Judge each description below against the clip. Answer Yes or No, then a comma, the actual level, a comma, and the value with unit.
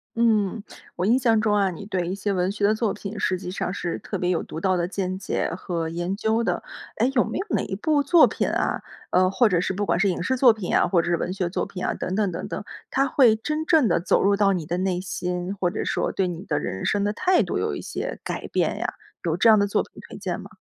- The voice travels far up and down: No, average, 3.5 semitones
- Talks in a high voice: Yes, high, 195 Hz